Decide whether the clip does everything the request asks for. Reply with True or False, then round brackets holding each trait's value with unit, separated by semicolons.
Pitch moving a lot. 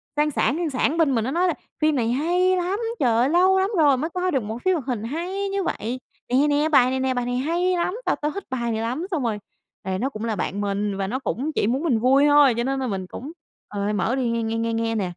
True (5.8 semitones)